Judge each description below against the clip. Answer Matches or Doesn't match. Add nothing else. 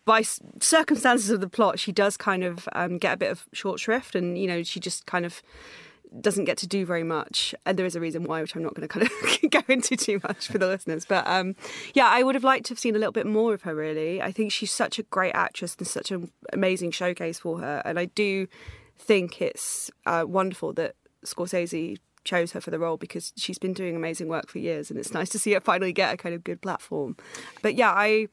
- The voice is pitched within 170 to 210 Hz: Matches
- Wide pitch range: Doesn't match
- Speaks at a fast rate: Matches